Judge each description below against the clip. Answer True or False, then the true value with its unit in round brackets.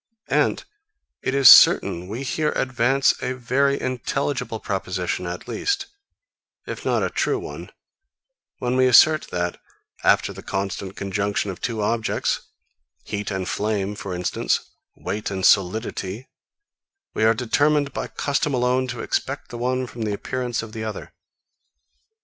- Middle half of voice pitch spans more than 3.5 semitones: True (4.6 semitones)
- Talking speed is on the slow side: False (145 wpm)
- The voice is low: True (115 Hz)